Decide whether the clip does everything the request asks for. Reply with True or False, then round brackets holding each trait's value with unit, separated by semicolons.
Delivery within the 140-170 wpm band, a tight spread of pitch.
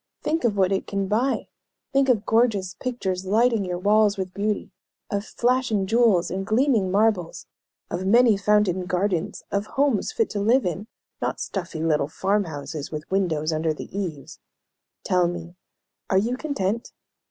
False (160 wpm; 3.8 semitones)